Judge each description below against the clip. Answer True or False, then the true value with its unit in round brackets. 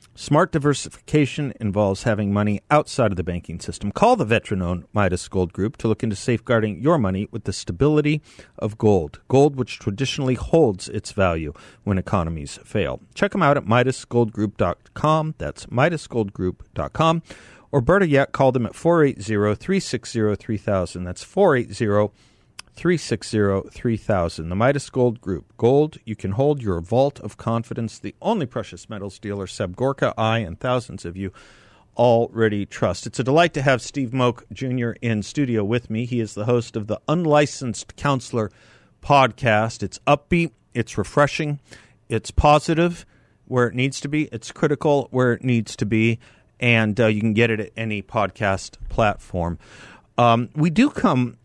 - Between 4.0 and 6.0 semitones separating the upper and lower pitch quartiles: True (4.6 semitones)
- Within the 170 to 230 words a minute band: False (160 wpm)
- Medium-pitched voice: False (115 Hz)